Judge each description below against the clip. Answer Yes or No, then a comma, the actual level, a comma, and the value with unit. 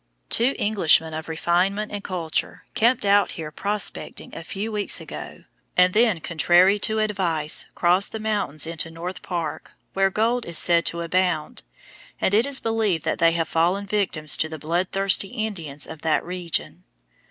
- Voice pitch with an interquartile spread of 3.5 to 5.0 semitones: Yes, average, 4.0 semitones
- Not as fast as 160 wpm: No, average, 165 wpm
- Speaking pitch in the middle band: Yes, medium, 180 Hz